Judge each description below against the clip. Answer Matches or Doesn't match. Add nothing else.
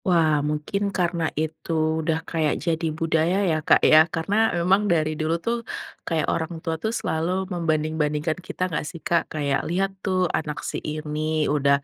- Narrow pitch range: Matches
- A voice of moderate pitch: Matches